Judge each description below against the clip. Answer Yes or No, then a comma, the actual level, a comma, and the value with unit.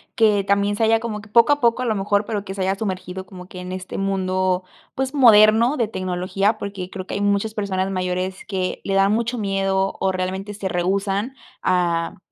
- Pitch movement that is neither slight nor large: No, narrow, 2.3 semitones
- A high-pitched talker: Yes, high, 195 Hz